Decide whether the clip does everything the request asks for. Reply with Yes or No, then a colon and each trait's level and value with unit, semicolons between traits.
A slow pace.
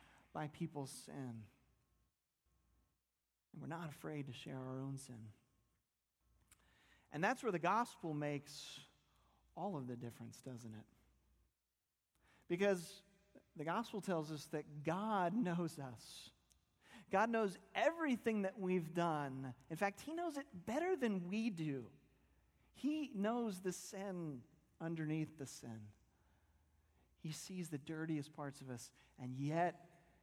Yes: slow, 125 wpm